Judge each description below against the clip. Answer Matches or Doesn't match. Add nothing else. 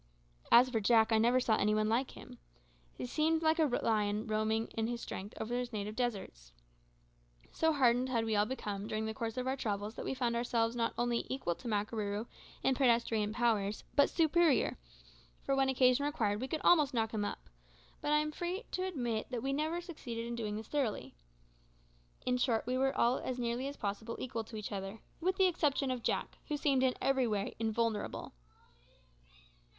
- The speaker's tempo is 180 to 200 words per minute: Matches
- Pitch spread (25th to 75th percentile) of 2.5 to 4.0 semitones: Matches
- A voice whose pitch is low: Doesn't match